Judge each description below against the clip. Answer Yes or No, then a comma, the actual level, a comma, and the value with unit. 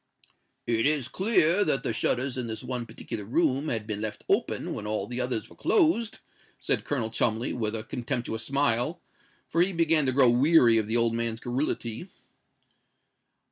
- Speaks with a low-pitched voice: Yes, low, 125 Hz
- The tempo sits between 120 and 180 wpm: Yes, average, 175 wpm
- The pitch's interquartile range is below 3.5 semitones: No, average, 4.7 semitones